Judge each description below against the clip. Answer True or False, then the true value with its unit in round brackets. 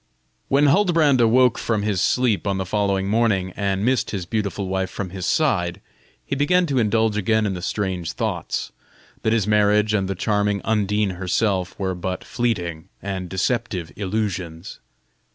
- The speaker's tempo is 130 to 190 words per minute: True (160 wpm)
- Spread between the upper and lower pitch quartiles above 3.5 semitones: False (3.1 semitones)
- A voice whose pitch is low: True (105 Hz)